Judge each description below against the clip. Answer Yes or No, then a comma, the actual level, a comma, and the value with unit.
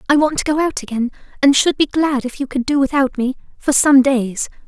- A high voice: Yes, very high, 270 Hz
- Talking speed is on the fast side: Yes, fast, 245 wpm